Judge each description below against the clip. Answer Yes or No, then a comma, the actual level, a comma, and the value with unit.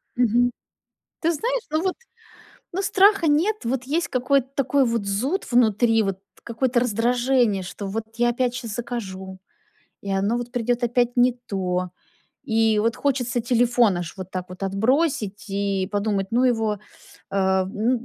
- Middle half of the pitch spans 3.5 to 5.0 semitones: Yes, average, 4.0 semitones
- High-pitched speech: Yes, high, 235 Hz